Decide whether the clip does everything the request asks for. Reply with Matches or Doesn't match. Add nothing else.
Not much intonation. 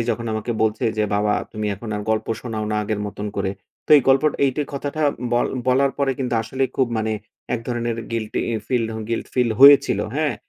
Doesn't match